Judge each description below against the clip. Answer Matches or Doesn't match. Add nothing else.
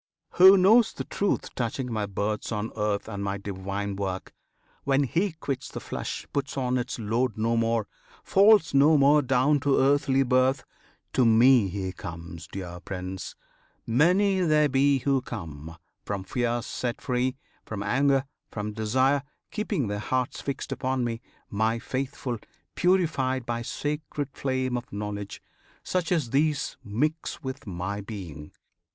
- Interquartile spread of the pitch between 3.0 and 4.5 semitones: Doesn't match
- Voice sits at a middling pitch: Doesn't match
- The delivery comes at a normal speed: Matches